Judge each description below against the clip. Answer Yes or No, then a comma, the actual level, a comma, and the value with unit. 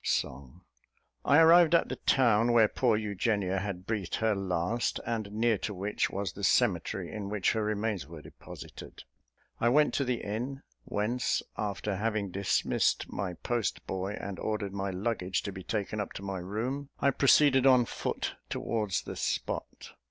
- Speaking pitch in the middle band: No, low, 105 Hz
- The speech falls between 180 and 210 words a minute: No, average, 165 wpm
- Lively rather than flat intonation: No, average, 3.4 semitones